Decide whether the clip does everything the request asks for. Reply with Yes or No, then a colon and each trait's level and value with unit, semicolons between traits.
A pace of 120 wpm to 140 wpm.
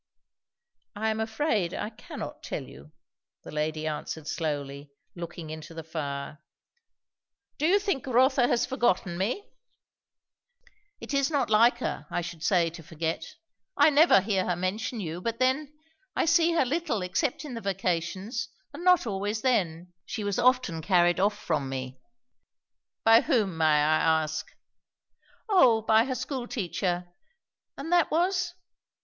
No: average, 150 wpm